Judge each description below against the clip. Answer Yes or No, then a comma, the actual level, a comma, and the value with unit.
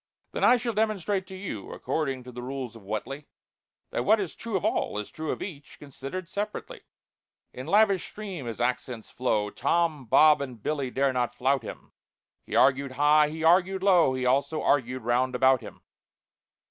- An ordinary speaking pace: Yes, average, 180 wpm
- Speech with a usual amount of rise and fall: No, wide, 6.0 semitones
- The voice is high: No, medium, 140 Hz